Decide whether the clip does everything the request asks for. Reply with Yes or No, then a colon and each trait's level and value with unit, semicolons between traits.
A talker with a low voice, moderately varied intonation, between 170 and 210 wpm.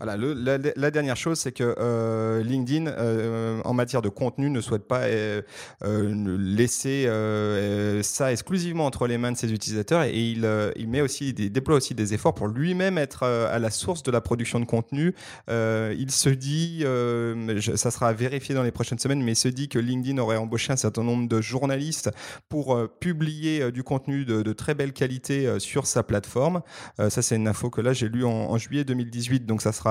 No: low, 120 Hz; average, 3.6 semitones; fast, 220 wpm